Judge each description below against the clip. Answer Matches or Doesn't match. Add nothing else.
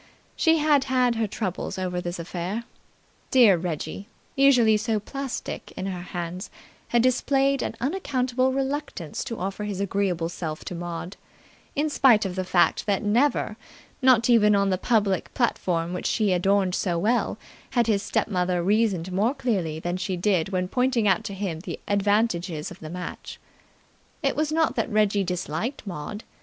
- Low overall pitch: Doesn't match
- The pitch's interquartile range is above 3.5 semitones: Matches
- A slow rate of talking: Doesn't match